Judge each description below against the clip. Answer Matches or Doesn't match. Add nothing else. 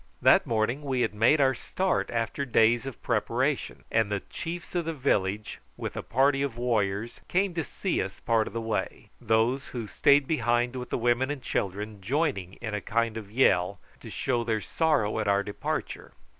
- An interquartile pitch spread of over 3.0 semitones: Matches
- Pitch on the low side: Matches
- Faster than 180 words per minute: Matches